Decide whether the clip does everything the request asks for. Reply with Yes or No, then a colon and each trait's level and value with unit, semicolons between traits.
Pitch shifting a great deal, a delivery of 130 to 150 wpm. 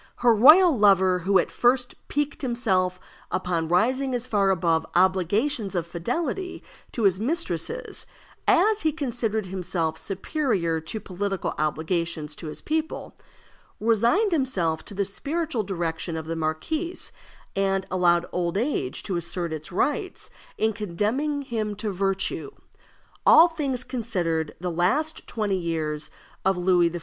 Yes: wide, 6.7 semitones; average, 140 wpm